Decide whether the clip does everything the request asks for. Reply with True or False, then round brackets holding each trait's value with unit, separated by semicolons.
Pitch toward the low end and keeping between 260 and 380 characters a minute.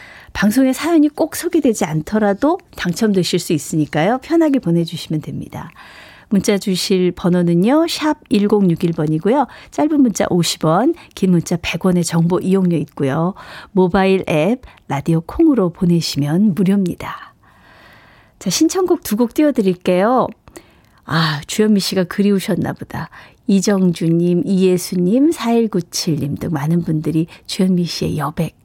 False (185 Hz; 280 characters per minute)